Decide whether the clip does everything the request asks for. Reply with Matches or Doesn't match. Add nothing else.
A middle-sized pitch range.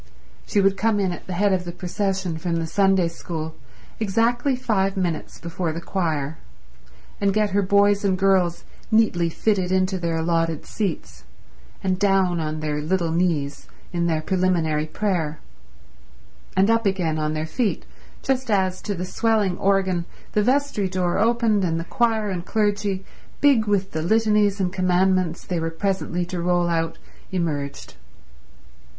Matches